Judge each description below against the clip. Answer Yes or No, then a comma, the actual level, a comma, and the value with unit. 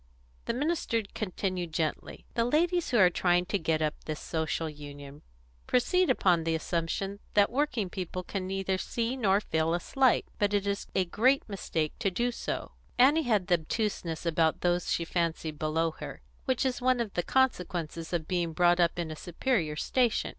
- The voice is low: No, medium, 185 Hz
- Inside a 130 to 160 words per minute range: No, average, 180 wpm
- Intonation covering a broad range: Yes, wide, 6.1 semitones